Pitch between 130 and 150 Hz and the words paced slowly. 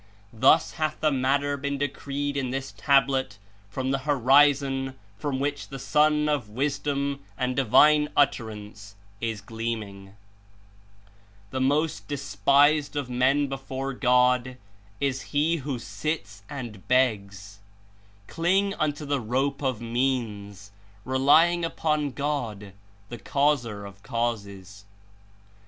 Yes: low, 135 Hz; slow, 115 wpm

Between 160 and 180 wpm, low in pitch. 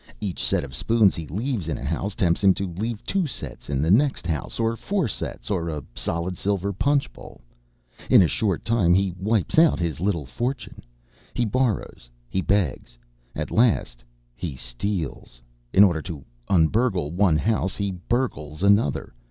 Yes: average, 175 wpm; very low, 95 Hz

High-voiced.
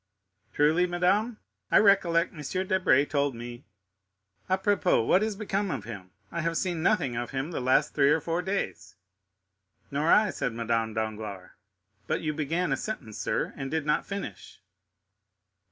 No: medium, 150 Hz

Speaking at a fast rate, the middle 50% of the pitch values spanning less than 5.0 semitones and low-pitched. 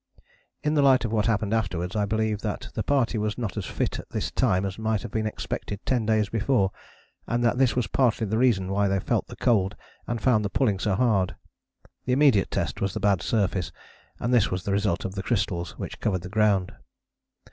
Yes: fast, 220 wpm; average, 3.3 semitones; low, 105 Hz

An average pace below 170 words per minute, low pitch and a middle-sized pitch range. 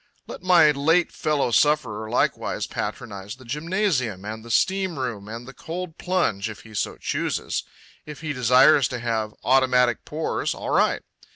No: average, 160 wpm; low, 130 Hz; wide, 5.7 semitones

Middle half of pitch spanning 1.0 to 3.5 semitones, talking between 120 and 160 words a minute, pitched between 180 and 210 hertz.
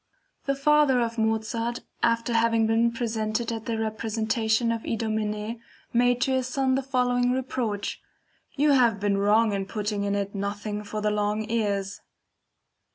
No: narrow, 2.5 semitones; average, 155 wpm; high, 225 Hz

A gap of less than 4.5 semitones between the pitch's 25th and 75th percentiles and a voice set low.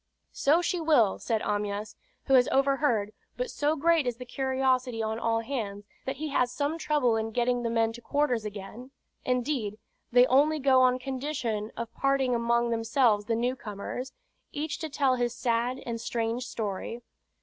No: average, 3.2 semitones; high, 245 Hz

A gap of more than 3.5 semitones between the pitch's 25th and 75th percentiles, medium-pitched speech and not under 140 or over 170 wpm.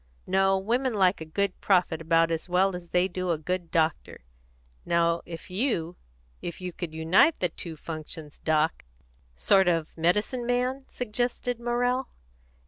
Yes: average, 4.3 semitones; medium, 180 Hz; average, 155 wpm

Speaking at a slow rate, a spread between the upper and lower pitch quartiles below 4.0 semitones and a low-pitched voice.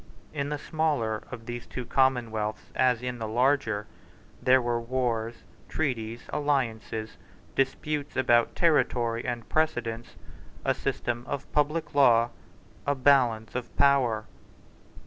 Yes: slow, 120 wpm; average, 3.5 semitones; low, 125 Hz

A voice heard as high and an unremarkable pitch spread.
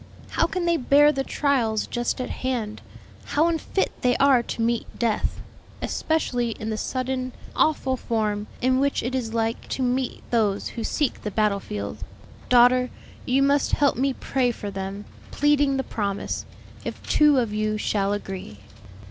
Yes: high, 245 Hz; average, 4.0 semitones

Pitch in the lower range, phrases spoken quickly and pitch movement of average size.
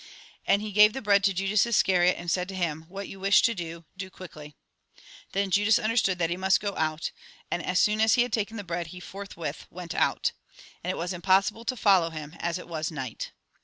No: medium, 185 Hz; fast, 235 wpm; average, 3.1 semitones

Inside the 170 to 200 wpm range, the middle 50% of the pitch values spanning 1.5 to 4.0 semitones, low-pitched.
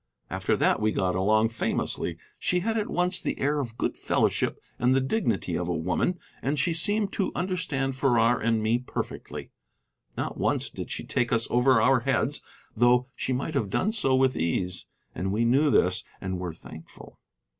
No: average, 185 wpm; average, 5.2 semitones; low, 125 Hz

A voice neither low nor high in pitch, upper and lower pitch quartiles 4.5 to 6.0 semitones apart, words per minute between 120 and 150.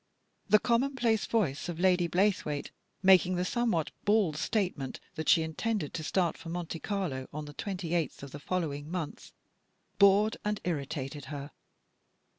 Yes: medium, 175 Hz; average, 4.9 semitones; average, 145 wpm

